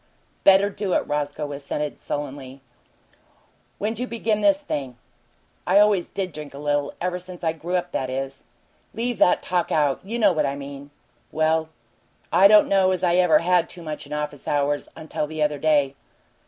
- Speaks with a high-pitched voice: No, medium, 160 Hz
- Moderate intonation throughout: Yes, average, 4.4 semitones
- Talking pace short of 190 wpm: Yes, average, 180 wpm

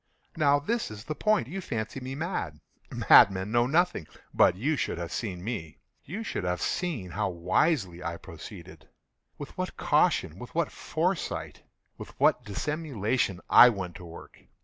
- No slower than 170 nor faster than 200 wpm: No, average, 150 wpm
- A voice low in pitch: Yes, low, 110 Hz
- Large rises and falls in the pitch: Yes, wide, 8.9 semitones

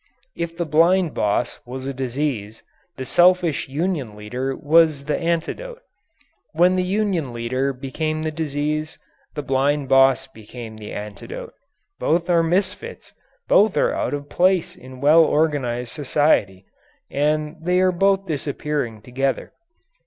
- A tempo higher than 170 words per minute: No, slow, 135 wpm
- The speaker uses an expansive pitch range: No, average, 4.5 semitones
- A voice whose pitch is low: No, medium, 150 Hz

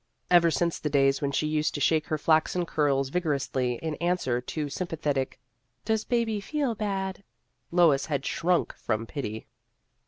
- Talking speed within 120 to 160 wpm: No, average, 175 wpm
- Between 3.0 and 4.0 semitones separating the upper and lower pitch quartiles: No, average, 4.6 semitones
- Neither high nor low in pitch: Yes, medium, 155 Hz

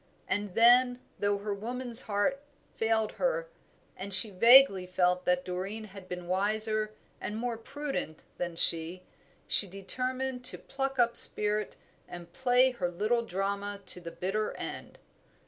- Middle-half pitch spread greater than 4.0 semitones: Yes, average, 4.7 semitones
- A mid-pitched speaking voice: No, high, 210 Hz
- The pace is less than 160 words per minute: Yes, average, 145 wpm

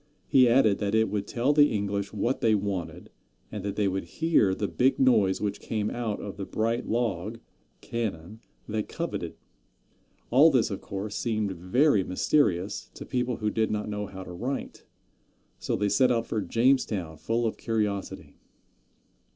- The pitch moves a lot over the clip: No, average, 3.2 semitones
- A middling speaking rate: Yes, average, 165 wpm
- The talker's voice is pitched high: No, low, 105 Hz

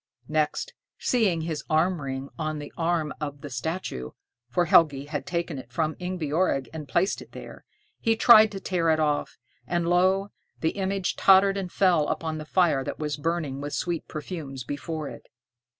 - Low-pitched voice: No, medium, 160 Hz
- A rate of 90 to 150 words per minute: No, average, 175 wpm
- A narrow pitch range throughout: No, average, 3.6 semitones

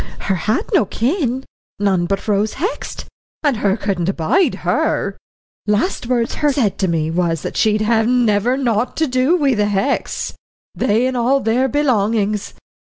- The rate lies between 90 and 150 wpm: No, average, 160 wpm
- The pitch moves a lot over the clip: No, average, 4.4 semitones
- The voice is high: Yes, high, 225 Hz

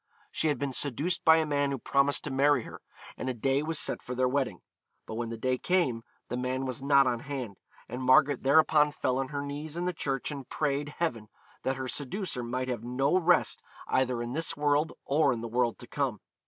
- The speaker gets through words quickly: Yes, fast, 220 wpm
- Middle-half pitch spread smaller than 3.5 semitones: Yes, average, 2.8 semitones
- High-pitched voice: No, low, 135 Hz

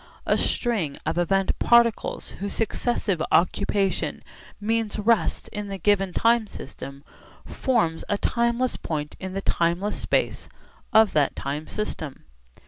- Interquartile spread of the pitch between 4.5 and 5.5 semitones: Yes, average, 4.9 semitones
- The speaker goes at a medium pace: No, slow, 130 wpm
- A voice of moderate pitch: No, high, 200 Hz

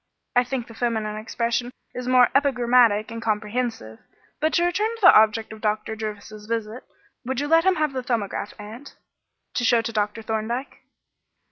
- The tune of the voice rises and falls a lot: No, average, 2.8 semitones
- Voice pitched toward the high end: Yes, high, 230 Hz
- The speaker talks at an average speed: Yes, average, 170 wpm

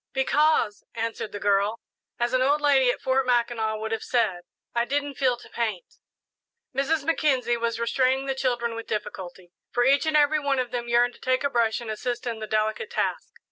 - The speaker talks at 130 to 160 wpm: No, average, 200 wpm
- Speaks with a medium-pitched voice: No, high, 245 Hz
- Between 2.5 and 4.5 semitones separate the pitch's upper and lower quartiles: Yes, average, 3.1 semitones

